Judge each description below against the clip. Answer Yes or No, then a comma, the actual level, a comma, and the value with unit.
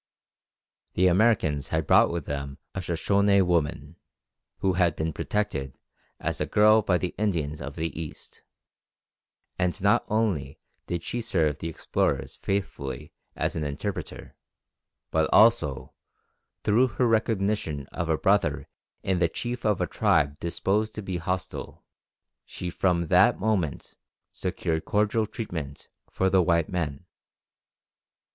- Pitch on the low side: Yes, very low, 90 Hz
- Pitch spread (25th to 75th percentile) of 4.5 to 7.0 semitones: Yes, average, 4.9 semitones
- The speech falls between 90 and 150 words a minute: Yes, slow, 135 wpm